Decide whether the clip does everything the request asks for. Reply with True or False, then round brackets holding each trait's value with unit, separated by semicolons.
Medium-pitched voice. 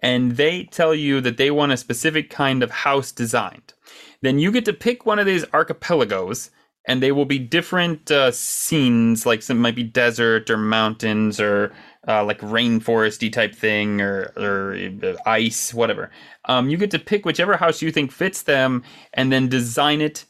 False (130 Hz)